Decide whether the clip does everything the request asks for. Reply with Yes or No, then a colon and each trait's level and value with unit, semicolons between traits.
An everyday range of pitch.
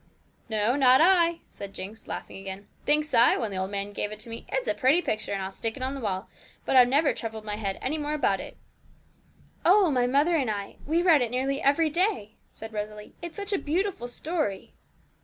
No: wide, 6.8 semitones